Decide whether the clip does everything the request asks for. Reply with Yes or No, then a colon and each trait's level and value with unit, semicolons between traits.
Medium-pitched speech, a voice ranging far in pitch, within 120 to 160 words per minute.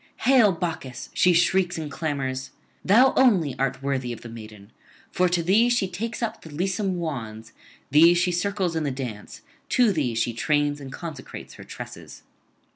No: medium, 160 Hz; wide, 6.1 semitones; average, 170 wpm